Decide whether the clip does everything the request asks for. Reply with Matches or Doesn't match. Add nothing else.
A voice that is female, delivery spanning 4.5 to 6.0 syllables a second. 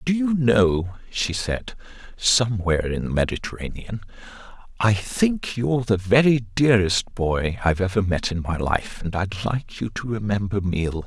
Doesn't match